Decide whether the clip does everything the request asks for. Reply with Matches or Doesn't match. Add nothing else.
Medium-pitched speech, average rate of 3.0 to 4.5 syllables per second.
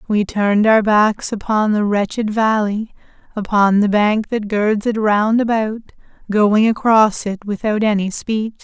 Doesn't match